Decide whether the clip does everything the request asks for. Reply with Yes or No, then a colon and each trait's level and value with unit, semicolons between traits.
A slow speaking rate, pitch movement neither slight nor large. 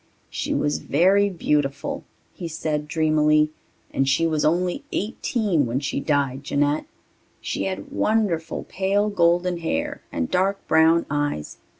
Yes: slow, 130 wpm; average, 4.0 semitones